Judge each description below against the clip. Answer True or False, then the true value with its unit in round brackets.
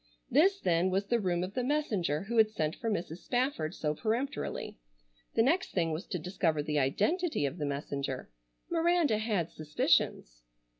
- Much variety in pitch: True (7.9 semitones)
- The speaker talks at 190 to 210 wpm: False (165 wpm)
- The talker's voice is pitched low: False (190 Hz)